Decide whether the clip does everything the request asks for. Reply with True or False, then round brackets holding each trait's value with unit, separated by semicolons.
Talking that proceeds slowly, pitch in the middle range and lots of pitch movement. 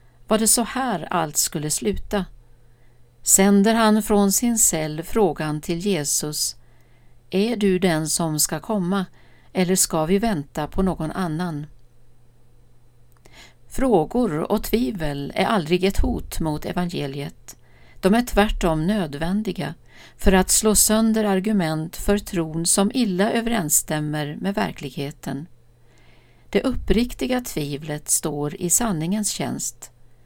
True (120 wpm; 170 Hz; 6.0 semitones)